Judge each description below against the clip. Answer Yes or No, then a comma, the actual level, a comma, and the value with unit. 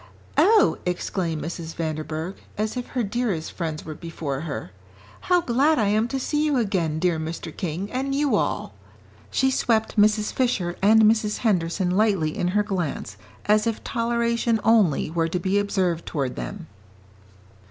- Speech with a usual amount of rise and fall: No, wide, 5.7 semitones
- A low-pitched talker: No, high, 200 Hz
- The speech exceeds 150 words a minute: Yes, average, 160 wpm